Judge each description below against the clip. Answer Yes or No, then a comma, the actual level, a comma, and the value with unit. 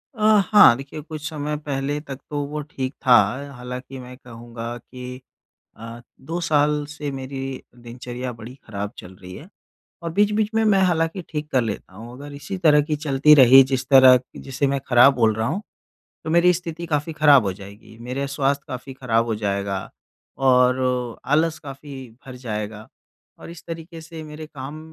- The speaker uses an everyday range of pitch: Yes, average, 3.8 semitones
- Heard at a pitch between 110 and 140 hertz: Yes, low, 135 Hz